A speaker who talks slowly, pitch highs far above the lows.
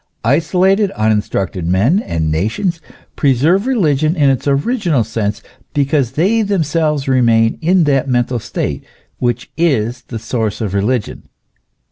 Yes: slow, 125 wpm; wide, 6.6 semitones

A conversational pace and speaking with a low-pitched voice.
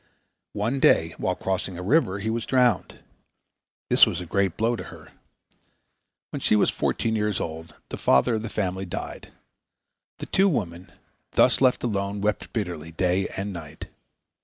Yes: average, 160 wpm; low, 100 Hz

